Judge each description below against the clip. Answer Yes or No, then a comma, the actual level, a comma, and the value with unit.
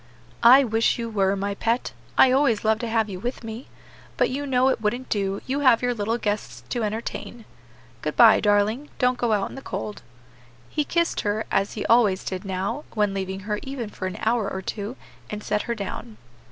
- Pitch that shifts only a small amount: No, average, 3.3 semitones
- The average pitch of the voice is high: Yes, high, 220 Hz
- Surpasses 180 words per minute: Yes, fast, 205 wpm